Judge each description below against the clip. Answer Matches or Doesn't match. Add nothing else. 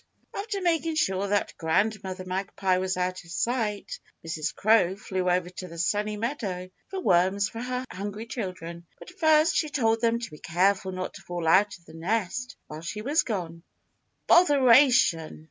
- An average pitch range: Matches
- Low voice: Doesn't match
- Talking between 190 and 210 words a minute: Doesn't match